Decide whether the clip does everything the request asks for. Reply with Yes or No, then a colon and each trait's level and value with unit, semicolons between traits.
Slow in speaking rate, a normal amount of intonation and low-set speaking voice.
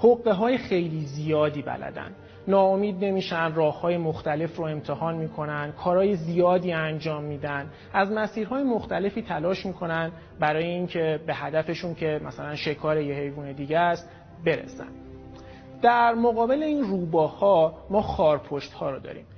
No: slow, 130 wpm; average, 4.3 semitones; medium, 165 Hz